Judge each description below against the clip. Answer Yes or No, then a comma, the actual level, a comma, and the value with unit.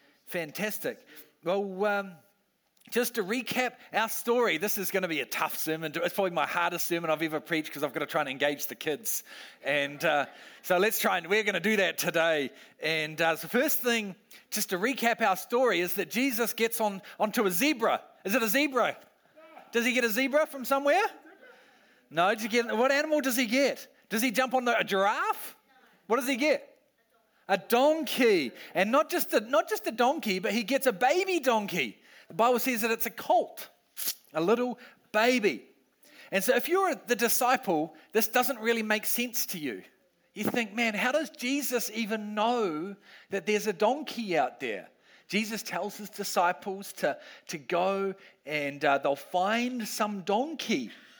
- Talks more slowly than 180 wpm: No, average, 190 wpm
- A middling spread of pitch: Yes, average, 4.7 semitones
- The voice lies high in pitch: Yes, high, 225 Hz